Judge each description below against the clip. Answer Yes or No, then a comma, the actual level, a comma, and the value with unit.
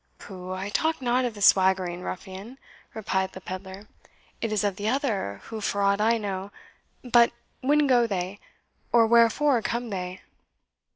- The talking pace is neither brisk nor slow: Yes, average, 160 wpm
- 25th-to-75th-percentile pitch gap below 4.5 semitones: Yes, average, 3.8 semitones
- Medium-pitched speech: No, high, 205 Hz